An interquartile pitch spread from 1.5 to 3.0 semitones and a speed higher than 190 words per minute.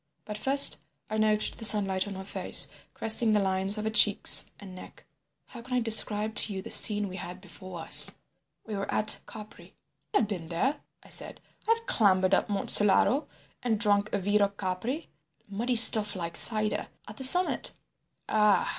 No: narrow, 2.5 semitones; average, 175 wpm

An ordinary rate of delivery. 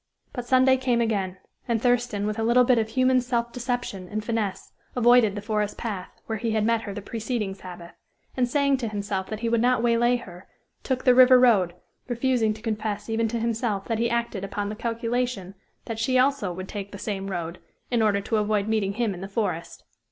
No: fast, 210 wpm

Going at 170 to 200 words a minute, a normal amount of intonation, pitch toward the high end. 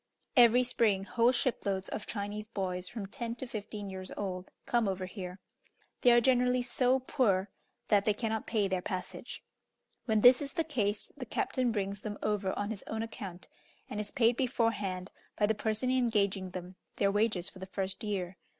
Yes: average, 180 wpm; average, 3.6 semitones; high, 210 Hz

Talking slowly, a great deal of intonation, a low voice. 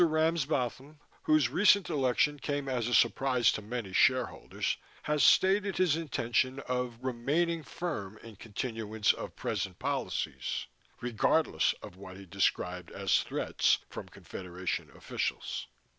Yes: slow, 125 wpm; wide, 5.7 semitones; low, 125 Hz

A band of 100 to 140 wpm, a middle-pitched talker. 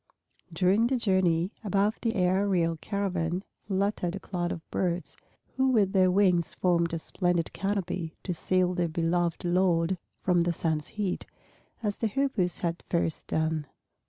No: average, 150 wpm; medium, 180 Hz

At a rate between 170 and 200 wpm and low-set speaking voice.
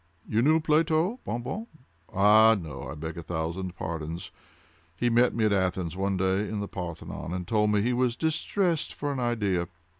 Yes: average, 180 wpm; low, 105 Hz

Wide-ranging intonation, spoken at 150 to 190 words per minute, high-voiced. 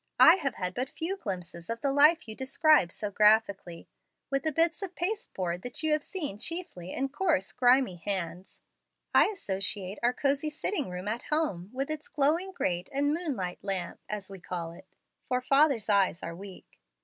Yes: wide, 8.4 semitones; average, 185 wpm; high, 245 Hz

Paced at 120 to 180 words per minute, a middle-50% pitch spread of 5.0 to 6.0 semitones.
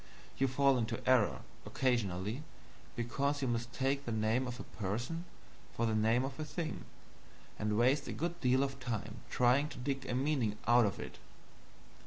No: average, 170 wpm; average, 3.3 semitones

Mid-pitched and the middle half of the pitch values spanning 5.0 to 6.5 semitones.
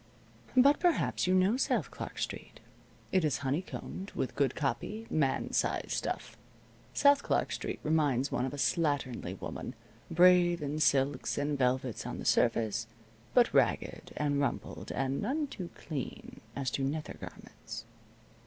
Yes: medium, 145 Hz; wide, 5.4 semitones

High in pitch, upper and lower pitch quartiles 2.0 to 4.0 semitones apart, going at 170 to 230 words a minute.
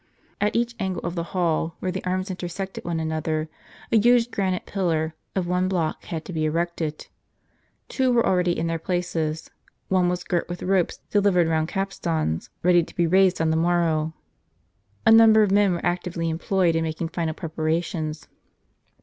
No: medium, 175 Hz; average, 2.7 semitones; average, 175 wpm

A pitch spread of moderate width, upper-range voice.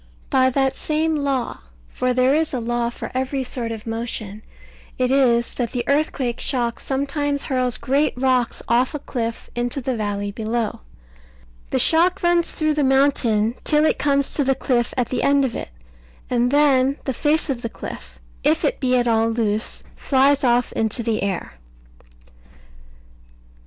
Yes: average, 3.1 semitones; very high, 255 Hz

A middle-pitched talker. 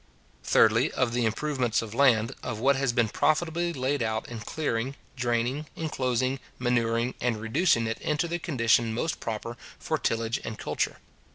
No: low, 120 Hz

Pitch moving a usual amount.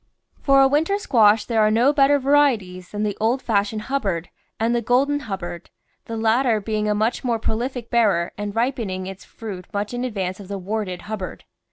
Yes: average, 3.8 semitones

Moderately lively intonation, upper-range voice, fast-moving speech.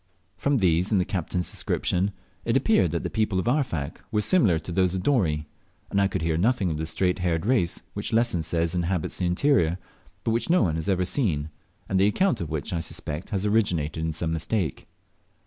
No: average, 4.5 semitones; very low, 90 Hz; fast, 210 wpm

